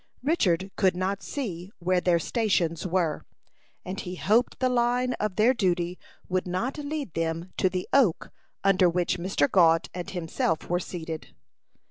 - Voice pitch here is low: No, medium, 185 Hz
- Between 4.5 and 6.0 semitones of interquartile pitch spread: No, average, 3.8 semitones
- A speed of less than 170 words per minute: Yes, average, 155 wpm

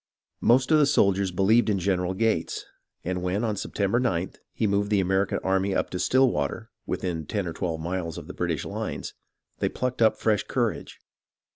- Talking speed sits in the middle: Yes, average, 180 wpm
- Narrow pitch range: No, average, 3.6 semitones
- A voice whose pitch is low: Yes, low, 100 Hz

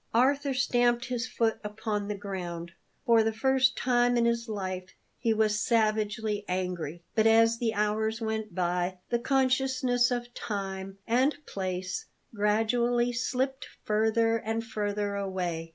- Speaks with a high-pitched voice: Yes, high, 220 Hz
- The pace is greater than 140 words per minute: No, slow, 135 wpm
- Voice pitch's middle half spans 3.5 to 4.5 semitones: No, average, 3.1 semitones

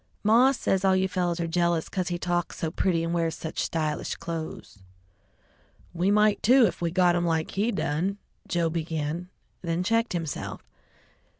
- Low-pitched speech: No, medium, 175 Hz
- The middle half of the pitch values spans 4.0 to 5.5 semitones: No, narrow, 2.5 semitones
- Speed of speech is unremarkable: Yes, average, 170 wpm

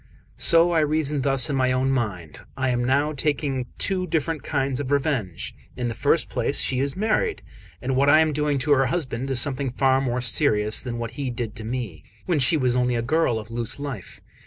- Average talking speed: No, fast, 215 wpm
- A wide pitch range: No, average, 3.3 semitones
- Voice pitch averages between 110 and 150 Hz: Yes, low, 135 Hz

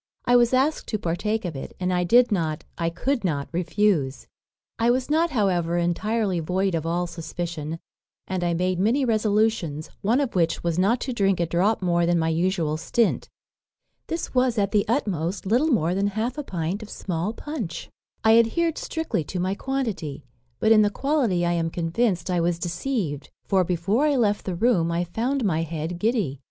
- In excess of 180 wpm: Yes, average, 190 wpm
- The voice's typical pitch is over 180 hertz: Yes, high, 190 Hz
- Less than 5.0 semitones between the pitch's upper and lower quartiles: No, average, 5.3 semitones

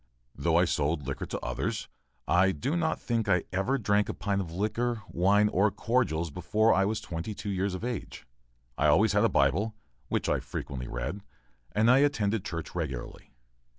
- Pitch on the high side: No, low, 100 Hz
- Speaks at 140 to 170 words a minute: No, average, 185 wpm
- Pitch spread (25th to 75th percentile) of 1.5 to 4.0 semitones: No, average, 4.6 semitones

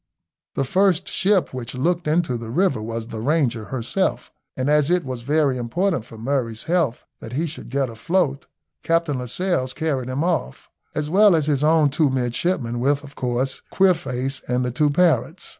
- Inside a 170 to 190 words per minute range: Yes, average, 175 wpm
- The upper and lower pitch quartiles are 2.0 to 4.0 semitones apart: No, average, 5.0 semitones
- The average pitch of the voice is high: No, medium, 140 Hz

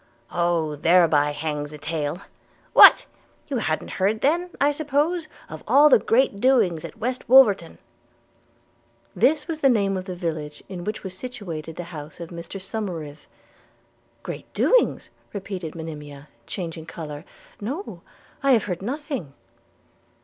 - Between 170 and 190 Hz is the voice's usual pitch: Yes, medium, 185 Hz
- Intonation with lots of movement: Yes, wide, 8.0 semitones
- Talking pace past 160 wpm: No, average, 150 wpm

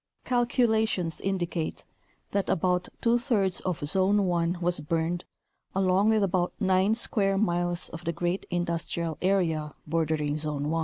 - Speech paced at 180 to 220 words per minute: No, average, 145 wpm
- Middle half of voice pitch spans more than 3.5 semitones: No, average, 2.9 semitones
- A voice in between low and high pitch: Yes, medium, 175 Hz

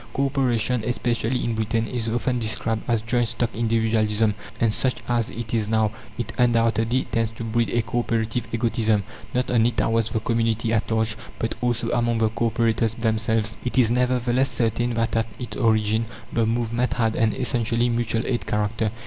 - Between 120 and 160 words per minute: No, average, 180 wpm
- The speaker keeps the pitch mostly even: Yes, narrow, 1.3 semitones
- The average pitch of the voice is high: No, low, 115 Hz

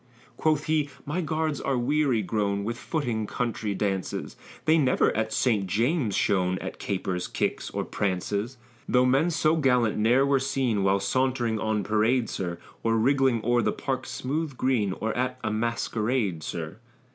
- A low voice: Yes, low, 120 Hz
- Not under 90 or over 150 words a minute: No, average, 160 wpm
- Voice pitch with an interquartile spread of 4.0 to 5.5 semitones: Yes, average, 4.5 semitones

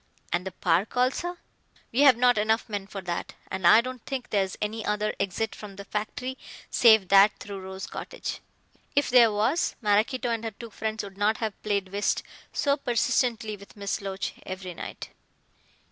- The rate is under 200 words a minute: Yes, average, 175 wpm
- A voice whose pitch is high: Yes, high, 210 Hz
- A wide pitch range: No, average, 3.3 semitones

